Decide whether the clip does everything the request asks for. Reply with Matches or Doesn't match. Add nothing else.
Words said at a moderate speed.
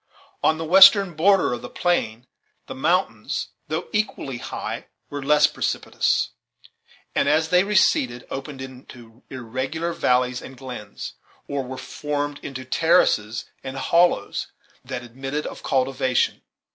Doesn't match